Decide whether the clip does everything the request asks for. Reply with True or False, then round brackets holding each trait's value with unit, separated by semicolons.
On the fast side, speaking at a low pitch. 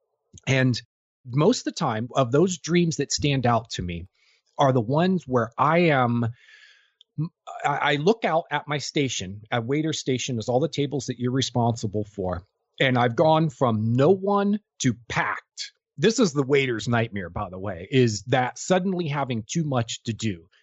False (175 wpm; 130 Hz)